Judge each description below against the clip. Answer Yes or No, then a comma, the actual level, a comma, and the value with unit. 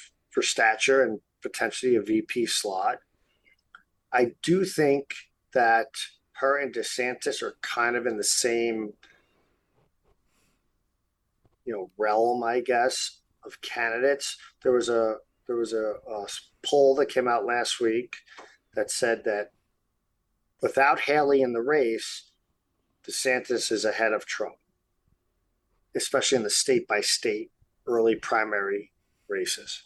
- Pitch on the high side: No, low, 125 Hz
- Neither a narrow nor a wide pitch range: No, wide, 6.7 semitones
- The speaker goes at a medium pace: No, slow, 125 wpm